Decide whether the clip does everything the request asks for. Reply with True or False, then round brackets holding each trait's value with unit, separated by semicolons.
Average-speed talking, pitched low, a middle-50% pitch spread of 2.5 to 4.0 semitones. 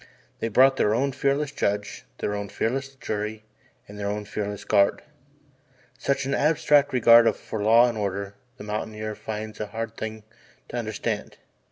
True (160 wpm; 110 Hz; 3.5 semitones)